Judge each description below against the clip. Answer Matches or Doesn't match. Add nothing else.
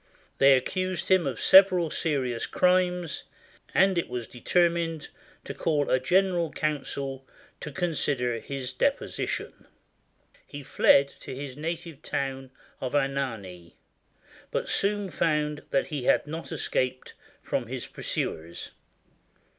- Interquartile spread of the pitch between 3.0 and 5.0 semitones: Matches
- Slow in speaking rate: Matches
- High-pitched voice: Doesn't match